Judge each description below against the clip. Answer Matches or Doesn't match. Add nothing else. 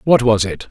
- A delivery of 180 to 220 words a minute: Doesn't match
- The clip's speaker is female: Doesn't match